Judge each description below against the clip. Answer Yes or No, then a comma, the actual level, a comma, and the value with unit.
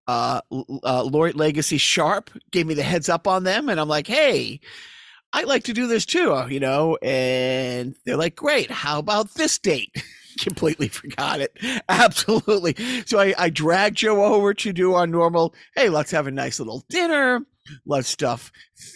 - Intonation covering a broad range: Yes, wide, 6.5 semitones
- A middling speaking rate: Yes, average, 175 wpm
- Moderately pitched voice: Yes, medium, 175 Hz